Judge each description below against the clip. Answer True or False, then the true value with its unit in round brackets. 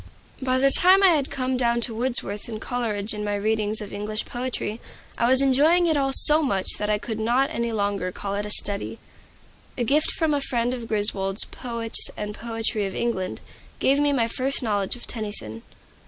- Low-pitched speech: False (230 Hz)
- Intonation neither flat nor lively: True (4.0 semitones)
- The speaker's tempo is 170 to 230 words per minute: True (195 wpm)